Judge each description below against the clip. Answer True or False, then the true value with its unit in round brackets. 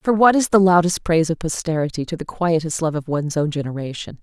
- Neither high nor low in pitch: True (165 Hz)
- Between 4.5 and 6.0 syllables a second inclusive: False (6.2 syllables/s)